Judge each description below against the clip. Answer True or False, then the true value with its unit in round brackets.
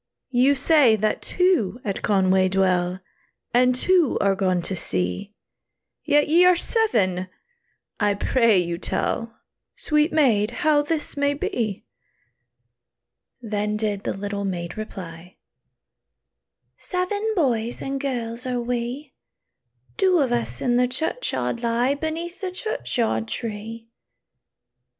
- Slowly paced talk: True (120 wpm)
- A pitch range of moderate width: False (6.5 semitones)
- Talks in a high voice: True (235 Hz)